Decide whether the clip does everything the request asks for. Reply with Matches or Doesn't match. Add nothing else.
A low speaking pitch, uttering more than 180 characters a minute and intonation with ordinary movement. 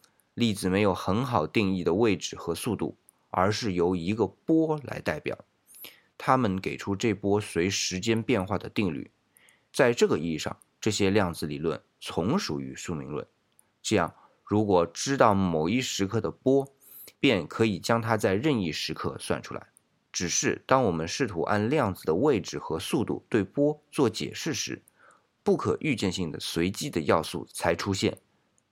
Matches